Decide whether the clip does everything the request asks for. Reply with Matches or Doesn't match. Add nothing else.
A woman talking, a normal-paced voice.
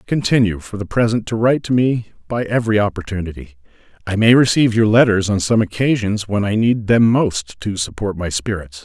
Doesn't match